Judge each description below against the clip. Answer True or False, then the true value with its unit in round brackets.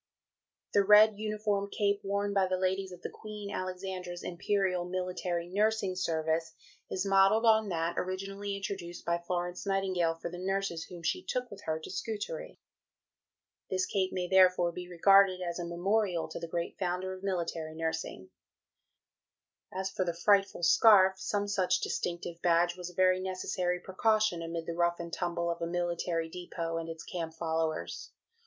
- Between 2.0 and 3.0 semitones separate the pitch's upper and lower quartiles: True (2.4 semitones)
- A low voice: False (185 Hz)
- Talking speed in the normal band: True (165 wpm)